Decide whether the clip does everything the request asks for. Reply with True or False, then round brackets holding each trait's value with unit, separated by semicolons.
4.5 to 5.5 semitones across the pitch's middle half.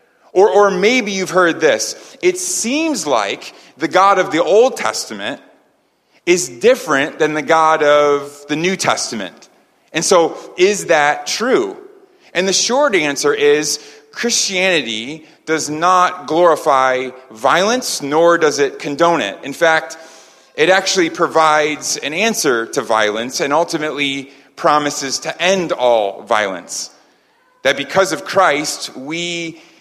True (5.2 semitones)